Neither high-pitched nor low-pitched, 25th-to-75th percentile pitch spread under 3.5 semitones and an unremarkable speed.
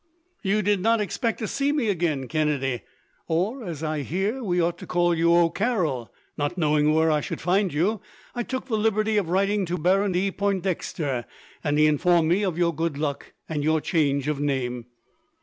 No: medium, 175 Hz; average, 4.9 semitones; average, 190 wpm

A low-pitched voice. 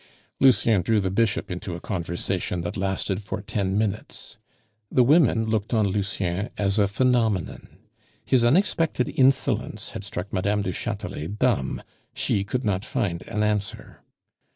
Yes: low, 105 Hz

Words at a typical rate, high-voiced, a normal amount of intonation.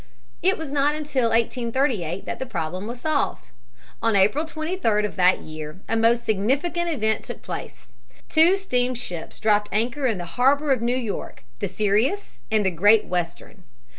No: average, 165 wpm; high, 230 Hz; wide, 5.8 semitones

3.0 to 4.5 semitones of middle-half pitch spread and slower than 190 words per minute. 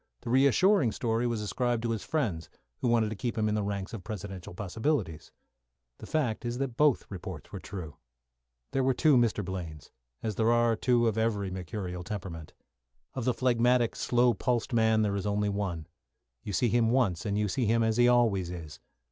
No: average, 3.7 semitones; average, 195 wpm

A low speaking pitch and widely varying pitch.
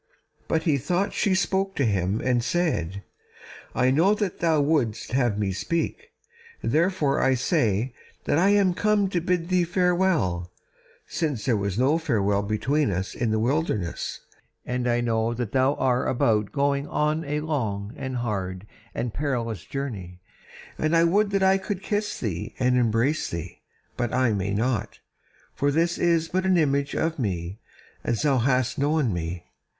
Yes: low, 130 Hz; wide, 7.3 semitones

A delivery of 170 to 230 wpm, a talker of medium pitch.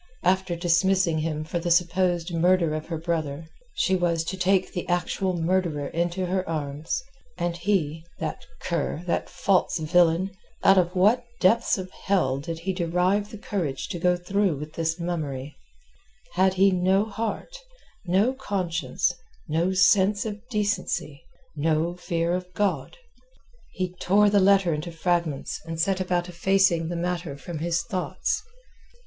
No: average, 145 wpm; medium, 175 Hz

